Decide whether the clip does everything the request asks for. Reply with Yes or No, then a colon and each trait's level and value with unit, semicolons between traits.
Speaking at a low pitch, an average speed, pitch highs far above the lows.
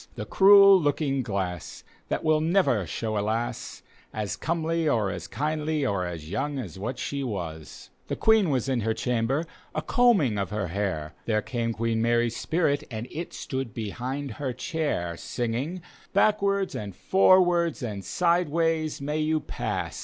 Yes: low, 130 Hz; average, 160 wpm; wide, 7.0 semitones